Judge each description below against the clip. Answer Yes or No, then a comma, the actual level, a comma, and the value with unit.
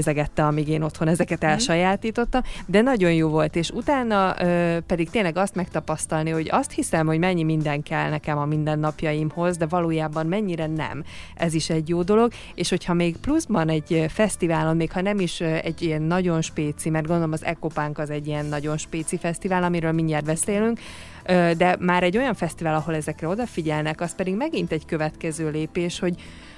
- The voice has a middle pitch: Yes, medium, 165 Hz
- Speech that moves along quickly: Yes, fast, 175 wpm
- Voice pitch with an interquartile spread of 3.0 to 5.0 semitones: No, narrow, 2.5 semitones